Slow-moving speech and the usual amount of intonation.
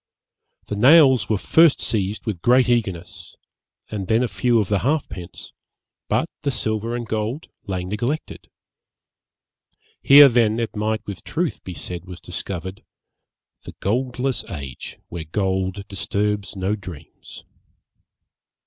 Yes: slow, 130 wpm; average, 4.2 semitones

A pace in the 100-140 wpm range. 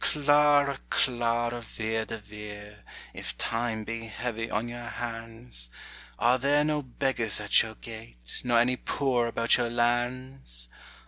Yes: slow, 135 wpm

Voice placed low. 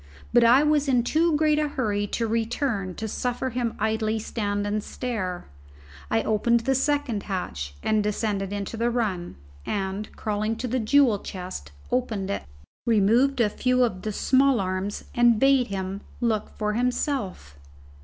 No: high, 220 Hz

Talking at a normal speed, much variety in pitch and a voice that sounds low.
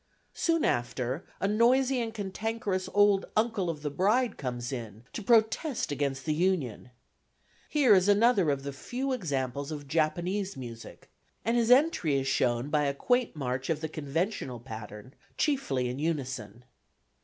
No: average, 155 wpm; wide, 8.6 semitones; medium, 160 Hz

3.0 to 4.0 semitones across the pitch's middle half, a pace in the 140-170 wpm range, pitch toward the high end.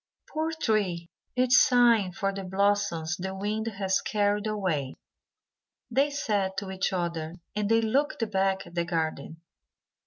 Yes: average, 3.5 semitones; average, 150 wpm; high, 195 Hz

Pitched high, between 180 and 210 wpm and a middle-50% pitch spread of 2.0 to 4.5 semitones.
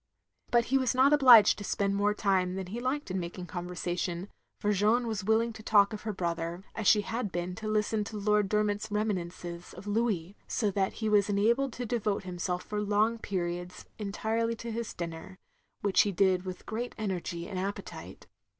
Yes: high, 205 Hz; average, 190 wpm; average, 3.2 semitones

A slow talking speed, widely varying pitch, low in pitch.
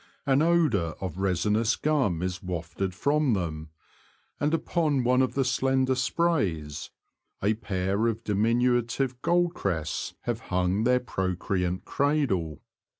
Yes: slow, 120 wpm; wide, 6.5 semitones; low, 115 Hz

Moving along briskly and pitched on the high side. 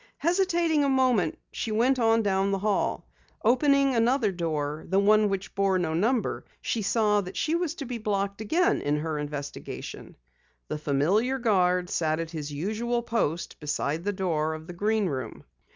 No: average, 170 wpm; high, 200 Hz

